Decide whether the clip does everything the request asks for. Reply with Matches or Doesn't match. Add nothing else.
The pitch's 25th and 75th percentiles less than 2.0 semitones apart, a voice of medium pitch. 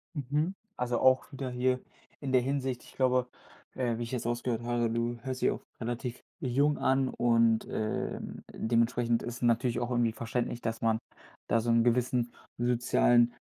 Doesn't match